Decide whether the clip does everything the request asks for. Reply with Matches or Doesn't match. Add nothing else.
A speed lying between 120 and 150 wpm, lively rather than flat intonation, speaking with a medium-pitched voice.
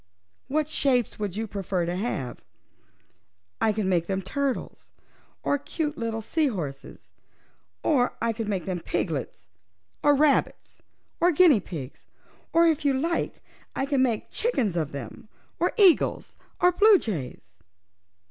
Doesn't match